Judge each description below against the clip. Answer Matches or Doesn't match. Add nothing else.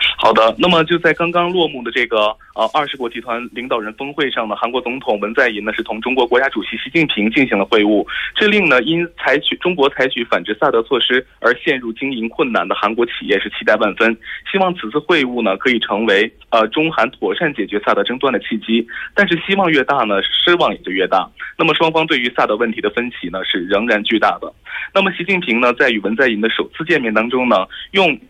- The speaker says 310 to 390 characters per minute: Matches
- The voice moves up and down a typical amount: Doesn't match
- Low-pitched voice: Matches